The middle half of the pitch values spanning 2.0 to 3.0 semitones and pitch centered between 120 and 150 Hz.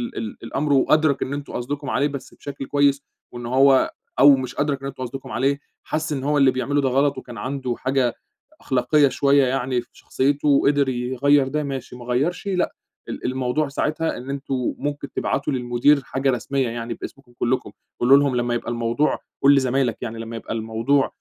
Yes: narrow, 2.4 semitones; low, 135 Hz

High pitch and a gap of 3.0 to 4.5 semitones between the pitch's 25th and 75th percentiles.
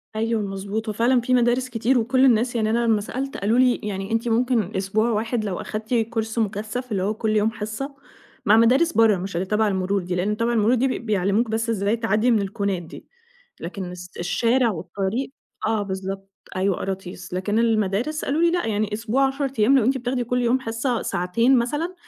Yes: high, 220 Hz; average, 3.4 semitones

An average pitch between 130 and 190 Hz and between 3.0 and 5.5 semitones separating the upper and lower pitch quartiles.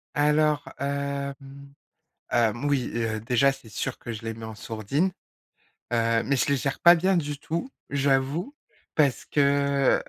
Yes: medium, 140 Hz; average, 3.7 semitones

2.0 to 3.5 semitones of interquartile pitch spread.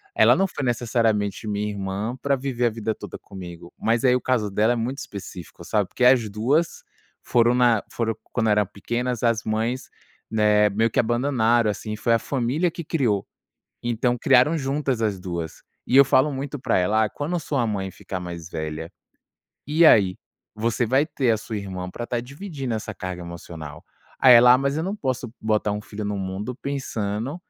No: average, 3.9 semitones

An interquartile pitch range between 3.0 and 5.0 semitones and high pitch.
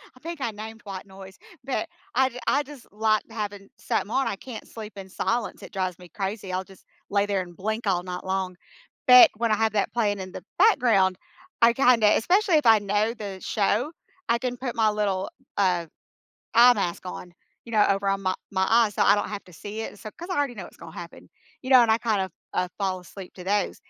Yes: average, 3.5 semitones; high, 210 Hz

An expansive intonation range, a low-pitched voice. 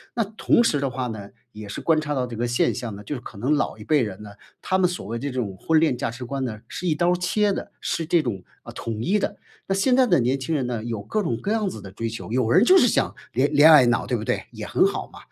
Yes: wide, 7.1 semitones; low, 130 Hz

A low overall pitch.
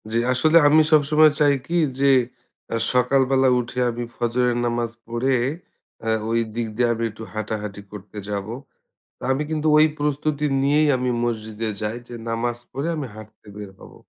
Yes: low, 120 Hz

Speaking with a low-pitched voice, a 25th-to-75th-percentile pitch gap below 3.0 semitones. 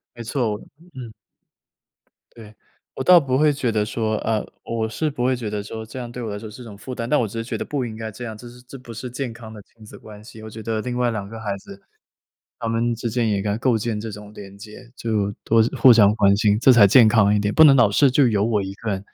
Yes: low, 115 Hz; narrow, 2.6 semitones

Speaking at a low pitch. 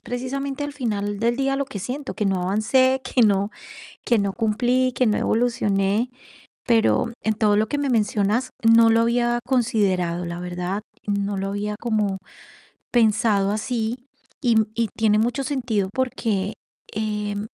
No: high, 220 Hz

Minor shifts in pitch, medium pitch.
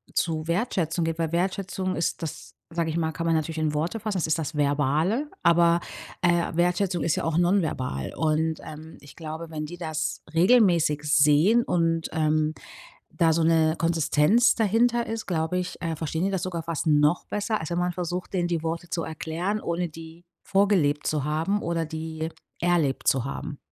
Yes: narrow, 2.1 semitones; medium, 165 Hz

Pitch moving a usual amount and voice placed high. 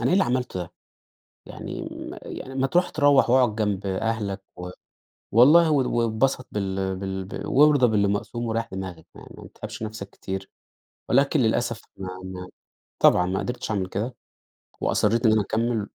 No: average, 4.5 semitones; low, 110 Hz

